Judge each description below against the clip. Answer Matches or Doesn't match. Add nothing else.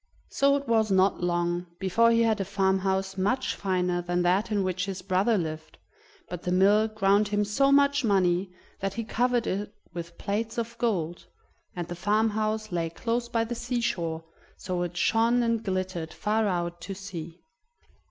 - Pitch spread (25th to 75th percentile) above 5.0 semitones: Doesn't match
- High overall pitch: Matches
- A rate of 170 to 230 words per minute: Matches